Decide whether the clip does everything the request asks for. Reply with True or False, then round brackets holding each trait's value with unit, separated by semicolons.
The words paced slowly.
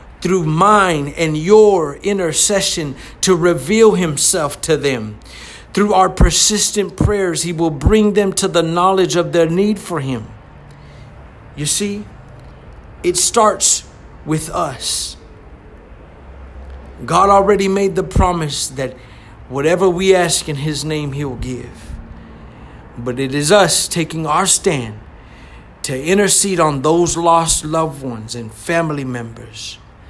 True (125 wpm)